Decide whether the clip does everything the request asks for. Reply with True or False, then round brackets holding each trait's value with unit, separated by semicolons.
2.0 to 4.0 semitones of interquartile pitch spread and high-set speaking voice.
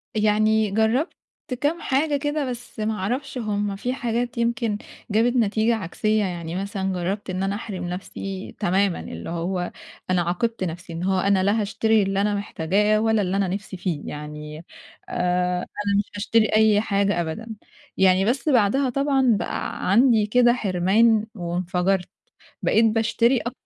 True (3.6 semitones; 205 Hz)